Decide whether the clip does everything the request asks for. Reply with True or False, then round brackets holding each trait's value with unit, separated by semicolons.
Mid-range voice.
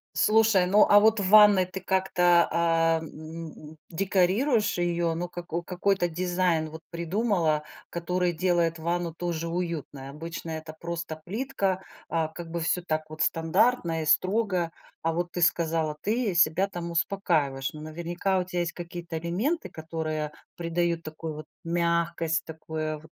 True (170 Hz)